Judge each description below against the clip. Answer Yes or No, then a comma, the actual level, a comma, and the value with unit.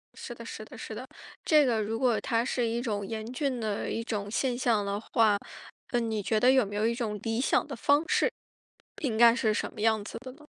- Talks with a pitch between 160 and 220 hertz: No, high, 230 Hz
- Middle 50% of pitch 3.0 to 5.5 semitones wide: No, narrow, 2.6 semitones